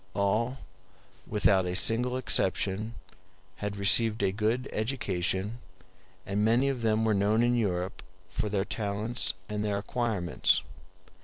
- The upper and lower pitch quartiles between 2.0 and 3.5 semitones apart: Yes, average, 2.8 semitones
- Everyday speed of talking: No, slow, 130 wpm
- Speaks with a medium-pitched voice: No, low, 105 Hz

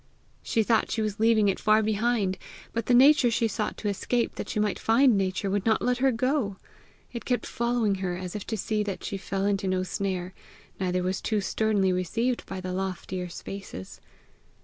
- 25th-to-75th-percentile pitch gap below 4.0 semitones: Yes, average, 3.3 semitones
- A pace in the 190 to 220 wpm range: Yes, average, 195 wpm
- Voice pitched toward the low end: No, high, 205 Hz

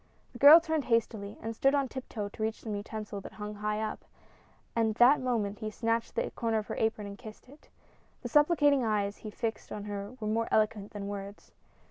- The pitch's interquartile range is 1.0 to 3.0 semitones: Yes, narrow, 2.6 semitones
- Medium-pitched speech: No, high, 220 Hz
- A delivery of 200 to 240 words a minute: Yes, fast, 205 wpm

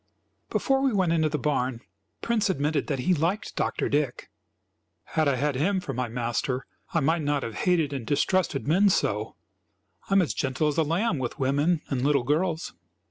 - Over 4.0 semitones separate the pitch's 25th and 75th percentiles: Yes, average, 4.6 semitones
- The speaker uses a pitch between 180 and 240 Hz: No, medium, 150 Hz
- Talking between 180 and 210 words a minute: Yes, average, 190 wpm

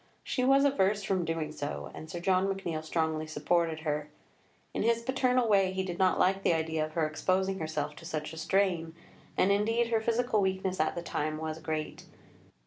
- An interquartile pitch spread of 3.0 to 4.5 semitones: Yes, average, 4.0 semitones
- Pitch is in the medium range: Yes, medium, 180 Hz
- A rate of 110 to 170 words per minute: No, average, 195 wpm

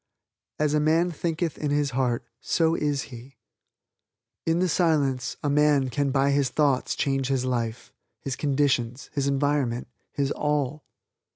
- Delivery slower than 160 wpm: Yes, average, 150 wpm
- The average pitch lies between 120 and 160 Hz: Yes, medium, 140 Hz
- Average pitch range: No, narrow, 2.3 semitones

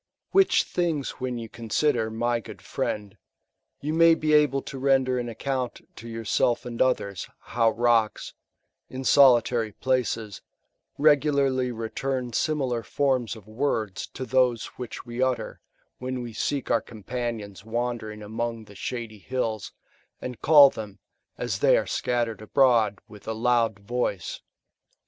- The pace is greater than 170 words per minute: No, average, 140 wpm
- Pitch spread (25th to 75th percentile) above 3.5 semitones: No, average, 2.8 semitones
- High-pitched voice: No, low, 120 Hz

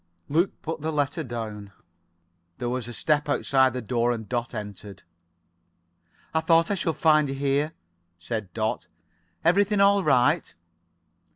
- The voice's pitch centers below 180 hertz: Yes, medium, 140 Hz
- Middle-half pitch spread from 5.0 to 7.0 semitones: Yes, average, 5.3 semitones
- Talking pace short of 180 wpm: Yes, slow, 135 wpm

